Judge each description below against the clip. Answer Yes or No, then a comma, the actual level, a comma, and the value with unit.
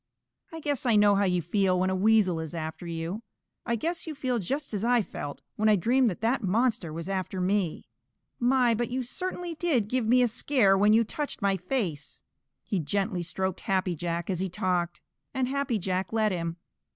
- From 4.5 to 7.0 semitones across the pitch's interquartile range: Yes, average, 5.2 semitones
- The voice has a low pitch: No, high, 205 Hz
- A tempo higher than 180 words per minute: Yes, average, 200 wpm